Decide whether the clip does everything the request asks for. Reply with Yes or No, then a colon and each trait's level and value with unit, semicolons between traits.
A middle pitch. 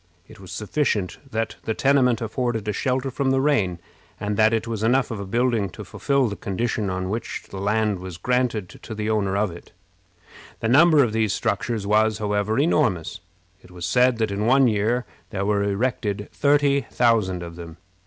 No: low, 110 Hz